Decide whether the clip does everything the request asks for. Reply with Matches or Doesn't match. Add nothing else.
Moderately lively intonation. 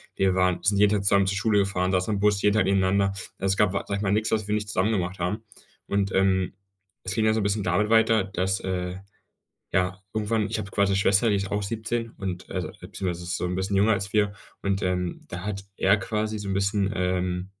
Doesn't match